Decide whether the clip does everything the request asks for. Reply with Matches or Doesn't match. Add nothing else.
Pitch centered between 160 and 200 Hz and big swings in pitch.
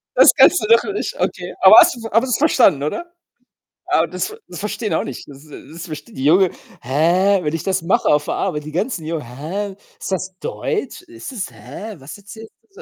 Matches